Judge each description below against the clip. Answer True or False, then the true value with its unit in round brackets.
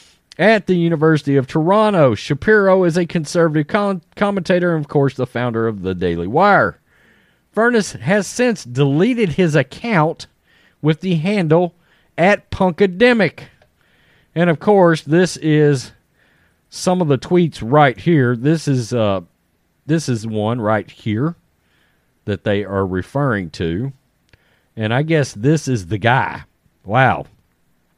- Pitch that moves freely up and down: True (6.8 semitones)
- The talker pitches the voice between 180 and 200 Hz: False (150 Hz)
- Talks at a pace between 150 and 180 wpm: False (135 wpm)